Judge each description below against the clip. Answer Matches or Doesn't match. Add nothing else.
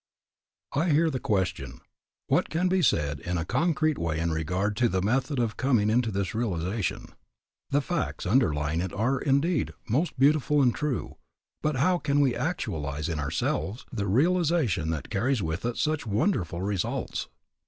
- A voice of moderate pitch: Doesn't match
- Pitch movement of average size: Doesn't match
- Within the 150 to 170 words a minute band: Matches